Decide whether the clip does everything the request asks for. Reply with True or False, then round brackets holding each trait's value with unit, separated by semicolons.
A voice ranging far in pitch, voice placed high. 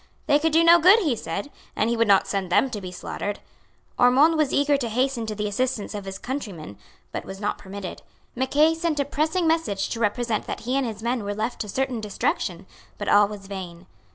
True (5.8 semitones; 230 Hz)